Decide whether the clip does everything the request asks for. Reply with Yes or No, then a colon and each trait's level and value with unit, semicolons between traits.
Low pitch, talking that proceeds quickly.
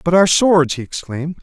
No: medium, 165 Hz; fast, 210 wpm